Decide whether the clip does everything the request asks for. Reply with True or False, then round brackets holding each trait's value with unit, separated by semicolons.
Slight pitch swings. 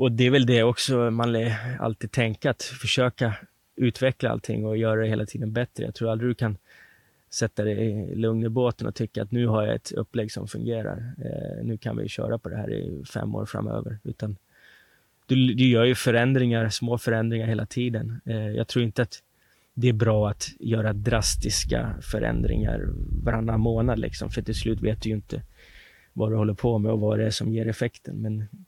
True (2.0 semitones)